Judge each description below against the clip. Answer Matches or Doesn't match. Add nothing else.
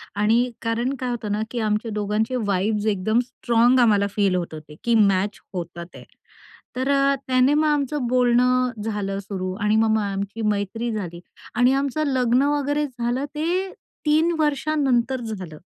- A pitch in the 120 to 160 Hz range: Doesn't match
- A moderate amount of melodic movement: Matches